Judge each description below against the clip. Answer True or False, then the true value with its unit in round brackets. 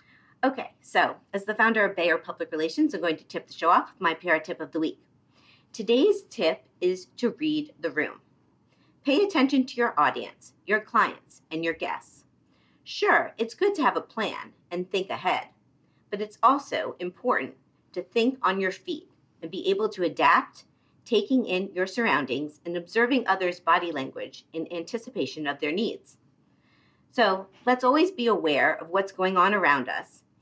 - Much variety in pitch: True (6.6 semitones)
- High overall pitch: True (215 Hz)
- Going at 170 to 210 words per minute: True (175 wpm)